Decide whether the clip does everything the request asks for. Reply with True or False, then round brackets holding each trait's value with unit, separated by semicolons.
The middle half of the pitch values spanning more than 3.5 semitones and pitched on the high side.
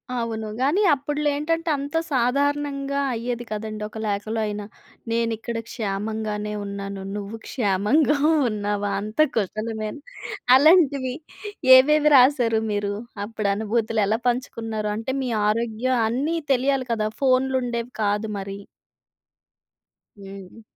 True (4.0 semitones; 230 Hz)